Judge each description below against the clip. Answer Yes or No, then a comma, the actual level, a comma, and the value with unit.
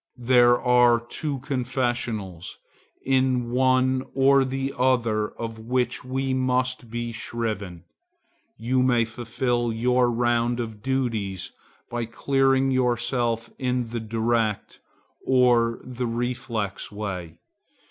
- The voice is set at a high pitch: No, low, 120 Hz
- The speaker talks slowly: Yes, slow, 110 wpm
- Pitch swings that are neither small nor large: No, narrow, 2.0 semitones